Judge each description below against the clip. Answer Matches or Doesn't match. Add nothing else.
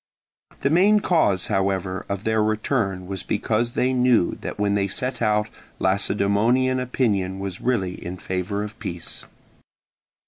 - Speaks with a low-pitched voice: Matches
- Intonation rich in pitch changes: Doesn't match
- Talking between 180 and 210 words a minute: Doesn't match